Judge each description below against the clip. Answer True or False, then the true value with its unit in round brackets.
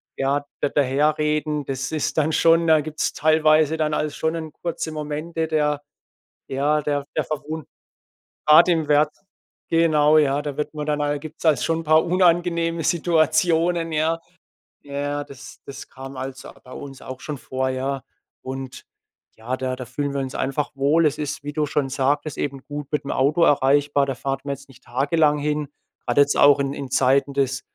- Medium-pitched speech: True (145 Hz)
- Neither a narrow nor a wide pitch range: False (2.3 semitones)